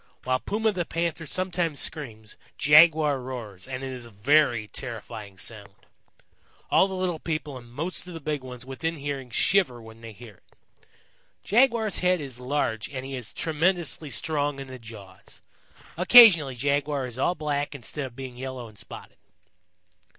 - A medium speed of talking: Yes, average, 165 wpm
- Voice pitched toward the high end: No, low, 135 Hz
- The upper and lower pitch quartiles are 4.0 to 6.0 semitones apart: Yes, average, 5.1 semitones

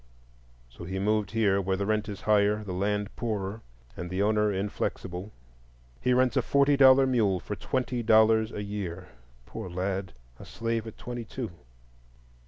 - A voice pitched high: No, low, 105 Hz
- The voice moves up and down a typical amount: Yes, average, 3.0 semitones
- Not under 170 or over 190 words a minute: No, average, 160 wpm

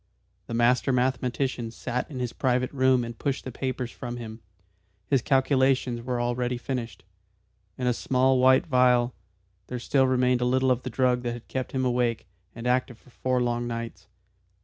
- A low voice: Yes, low, 125 Hz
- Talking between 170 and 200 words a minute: Yes, average, 175 wpm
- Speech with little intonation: Yes, narrow, 1.3 semitones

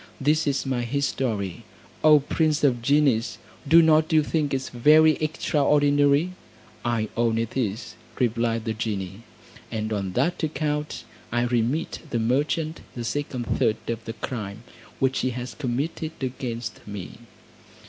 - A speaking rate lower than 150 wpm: Yes, average, 140 wpm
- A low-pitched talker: Yes, low, 130 Hz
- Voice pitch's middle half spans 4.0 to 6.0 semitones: Yes, average, 4.5 semitones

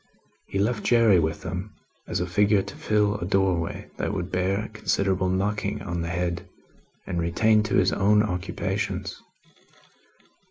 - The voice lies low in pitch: Yes, very low, 95 Hz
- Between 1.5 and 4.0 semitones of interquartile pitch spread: Yes, average, 2.8 semitones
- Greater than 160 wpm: No, average, 150 wpm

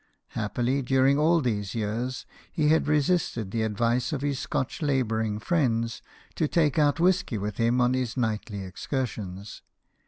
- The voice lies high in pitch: No, low, 125 Hz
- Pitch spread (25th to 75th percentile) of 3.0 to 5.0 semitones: Yes, average, 4.6 semitones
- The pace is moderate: Yes, average, 150 wpm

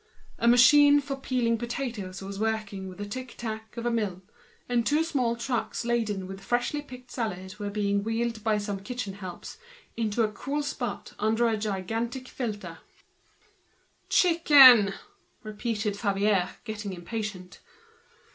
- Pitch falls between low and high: No, high, 225 Hz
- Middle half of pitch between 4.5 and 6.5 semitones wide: No, average, 3.2 semitones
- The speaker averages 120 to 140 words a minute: Yes, slow, 135 wpm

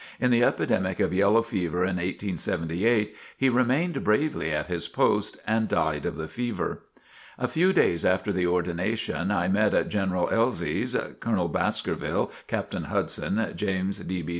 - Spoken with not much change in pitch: No, average, 4.2 semitones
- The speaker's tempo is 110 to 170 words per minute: Yes, average, 155 wpm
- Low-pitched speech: Yes, very low, 95 Hz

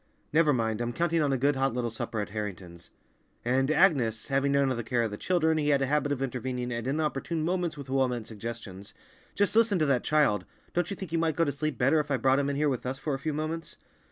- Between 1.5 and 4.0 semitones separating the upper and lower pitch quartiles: No, average, 4.4 semitones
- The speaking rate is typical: No, fast, 255 wpm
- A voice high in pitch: No, low, 135 Hz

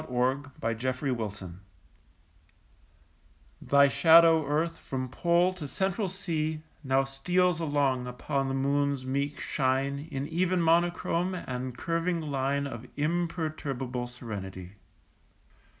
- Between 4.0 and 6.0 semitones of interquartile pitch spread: Yes, average, 4.3 semitones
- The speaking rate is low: Yes, slow, 110 wpm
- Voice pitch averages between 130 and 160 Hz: Yes, medium, 140 Hz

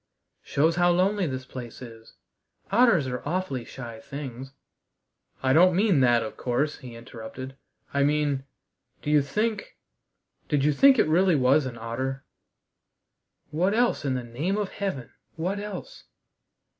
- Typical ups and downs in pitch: No, wide, 6.1 semitones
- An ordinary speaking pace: Yes, average, 150 wpm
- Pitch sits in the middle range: Yes, medium, 145 Hz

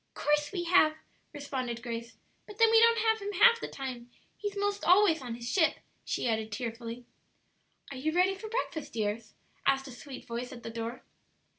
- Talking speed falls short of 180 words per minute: No, average, 185 wpm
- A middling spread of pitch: No, wide, 8.7 semitones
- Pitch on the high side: Yes, very high, 275 Hz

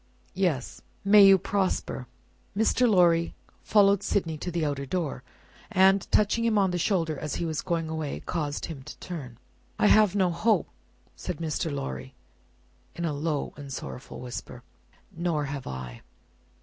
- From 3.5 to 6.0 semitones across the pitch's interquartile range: Yes, average, 5.0 semitones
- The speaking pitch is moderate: Yes, medium, 170 Hz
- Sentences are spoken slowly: No, average, 155 wpm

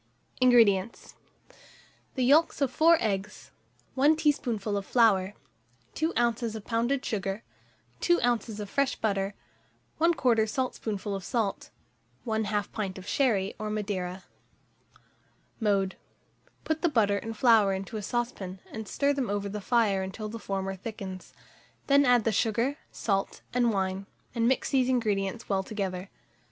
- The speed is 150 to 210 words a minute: No, average, 140 wpm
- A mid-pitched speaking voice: No, high, 220 Hz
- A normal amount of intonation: Yes, average, 3.9 semitones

